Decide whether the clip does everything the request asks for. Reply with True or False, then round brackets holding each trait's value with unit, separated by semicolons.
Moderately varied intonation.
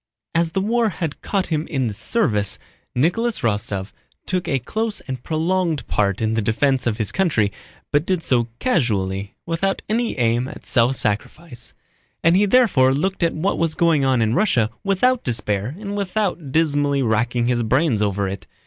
False (8.3 semitones)